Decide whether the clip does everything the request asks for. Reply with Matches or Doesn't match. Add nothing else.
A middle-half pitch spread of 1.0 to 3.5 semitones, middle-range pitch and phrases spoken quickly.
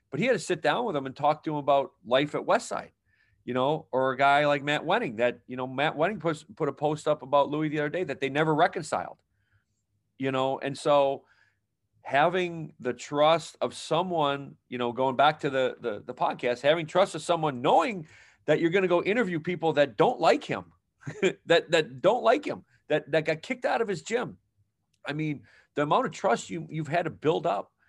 Matches